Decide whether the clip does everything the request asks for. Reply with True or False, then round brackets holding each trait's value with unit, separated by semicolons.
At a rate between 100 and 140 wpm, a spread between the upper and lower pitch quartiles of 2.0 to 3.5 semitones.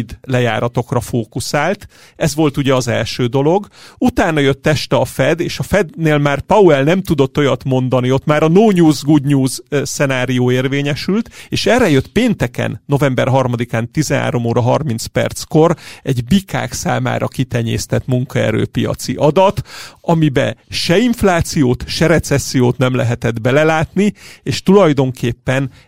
False (130 wpm; 4.0 semitones)